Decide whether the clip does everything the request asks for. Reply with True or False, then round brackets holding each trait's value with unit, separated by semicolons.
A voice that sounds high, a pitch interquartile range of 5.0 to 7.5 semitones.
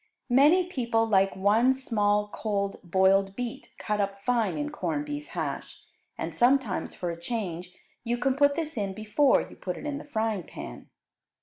True (225 Hz; 5.3 semitones)